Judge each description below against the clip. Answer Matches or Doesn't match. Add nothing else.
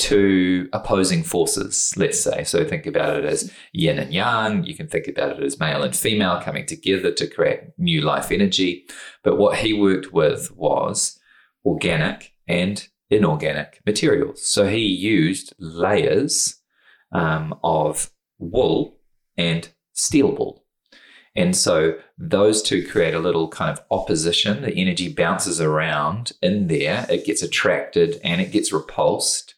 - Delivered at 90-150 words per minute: Matches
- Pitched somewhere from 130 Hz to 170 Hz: Doesn't match